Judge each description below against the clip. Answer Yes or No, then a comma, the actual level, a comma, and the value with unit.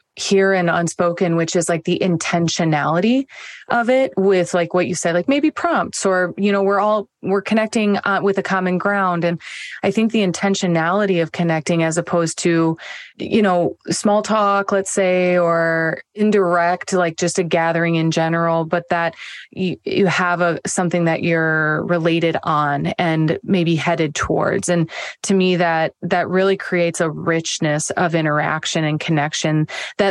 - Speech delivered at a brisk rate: No, average, 165 wpm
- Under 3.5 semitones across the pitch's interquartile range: Yes, average, 2.8 semitones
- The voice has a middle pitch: Yes, medium, 175 Hz